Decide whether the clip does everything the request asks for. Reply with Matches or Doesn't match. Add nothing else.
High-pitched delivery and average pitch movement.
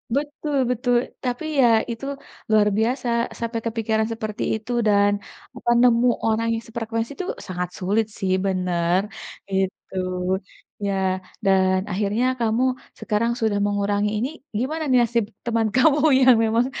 Matches